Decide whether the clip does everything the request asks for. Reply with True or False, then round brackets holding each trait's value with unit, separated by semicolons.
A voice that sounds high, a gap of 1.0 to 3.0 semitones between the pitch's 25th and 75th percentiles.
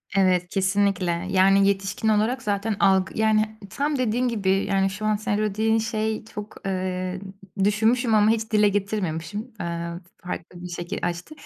True (200 Hz; 2.6 semitones)